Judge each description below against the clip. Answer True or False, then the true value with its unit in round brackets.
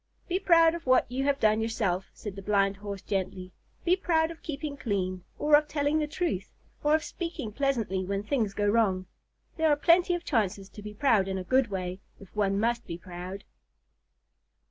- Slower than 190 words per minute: False (195 wpm)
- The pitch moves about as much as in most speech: False (7.3 semitones)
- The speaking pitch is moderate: False (220 Hz)